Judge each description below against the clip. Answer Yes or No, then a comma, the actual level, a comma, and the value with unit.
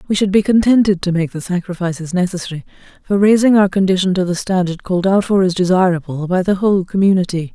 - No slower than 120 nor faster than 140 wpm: No, average, 200 wpm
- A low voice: No, medium, 185 Hz